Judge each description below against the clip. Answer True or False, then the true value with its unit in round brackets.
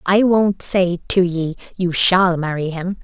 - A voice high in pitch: False (180 Hz)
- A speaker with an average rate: True (180 wpm)